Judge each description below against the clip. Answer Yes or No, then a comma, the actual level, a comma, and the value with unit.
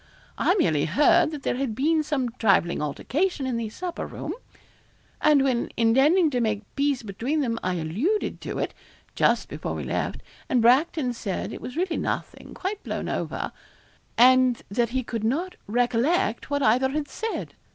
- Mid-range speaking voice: No, very high, 255 Hz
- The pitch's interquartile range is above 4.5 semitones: Yes, average, 4.9 semitones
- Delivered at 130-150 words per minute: No, average, 170 wpm